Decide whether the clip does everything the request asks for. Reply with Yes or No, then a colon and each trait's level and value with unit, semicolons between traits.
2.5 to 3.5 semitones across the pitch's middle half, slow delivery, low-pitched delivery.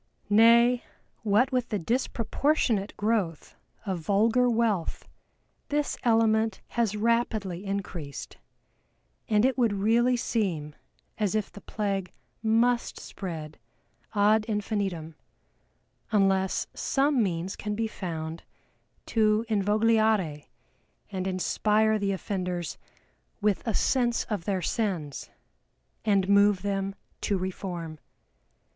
No: average, 3.2 semitones; slow, 105 wpm; high, 205 Hz